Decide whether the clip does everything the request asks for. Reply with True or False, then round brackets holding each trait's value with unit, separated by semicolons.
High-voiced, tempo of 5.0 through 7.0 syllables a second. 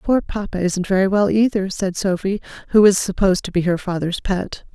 True (195 Hz; 5.4 syllables/s)